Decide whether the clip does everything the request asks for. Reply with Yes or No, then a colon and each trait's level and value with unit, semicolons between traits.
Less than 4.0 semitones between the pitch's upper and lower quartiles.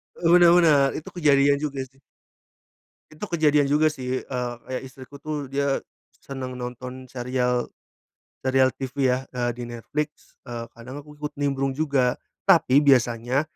Yes: narrow, 2.5 semitones